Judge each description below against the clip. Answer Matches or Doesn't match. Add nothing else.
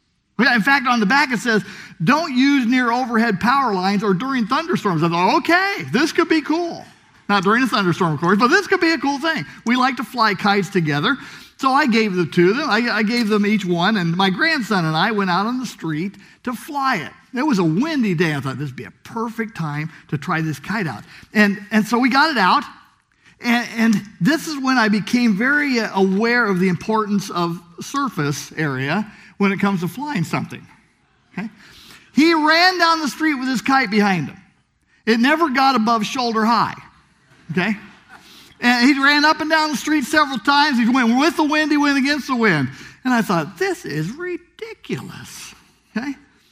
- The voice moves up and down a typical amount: Doesn't match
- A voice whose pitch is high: Matches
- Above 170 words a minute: Matches